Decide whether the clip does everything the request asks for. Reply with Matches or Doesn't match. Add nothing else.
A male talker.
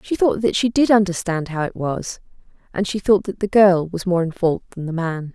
Doesn't match